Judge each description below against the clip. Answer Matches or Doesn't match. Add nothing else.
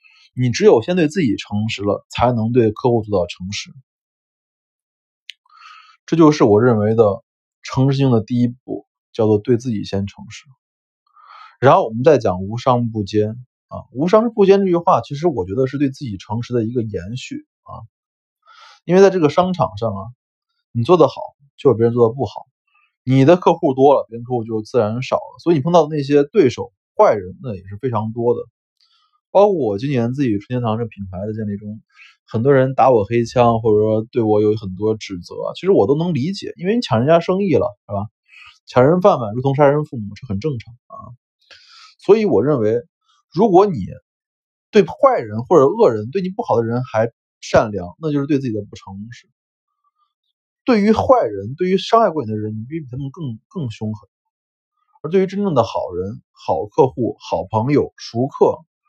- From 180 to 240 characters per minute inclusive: Doesn't match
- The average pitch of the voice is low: Matches